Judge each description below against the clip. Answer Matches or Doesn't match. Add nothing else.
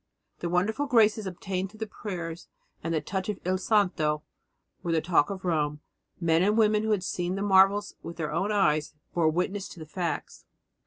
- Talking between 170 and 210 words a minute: Matches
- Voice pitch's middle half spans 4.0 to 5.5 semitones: Doesn't match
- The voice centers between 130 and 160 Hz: Doesn't match